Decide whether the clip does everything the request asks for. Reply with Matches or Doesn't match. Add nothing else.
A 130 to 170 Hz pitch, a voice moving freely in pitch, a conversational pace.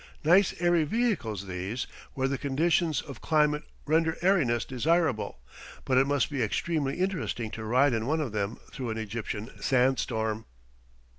Matches